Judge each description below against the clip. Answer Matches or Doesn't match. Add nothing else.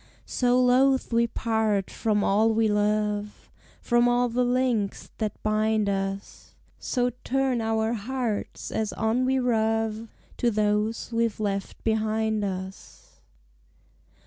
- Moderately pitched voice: Doesn't match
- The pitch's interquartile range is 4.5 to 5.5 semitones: Doesn't match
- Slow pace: Matches